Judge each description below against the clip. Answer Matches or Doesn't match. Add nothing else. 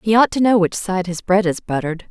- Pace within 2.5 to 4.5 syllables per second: Doesn't match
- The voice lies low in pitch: Doesn't match